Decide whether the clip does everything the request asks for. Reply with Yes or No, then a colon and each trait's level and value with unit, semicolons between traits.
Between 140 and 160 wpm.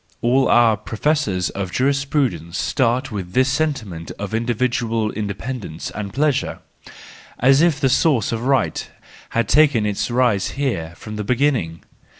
Yes: average, 145 wpm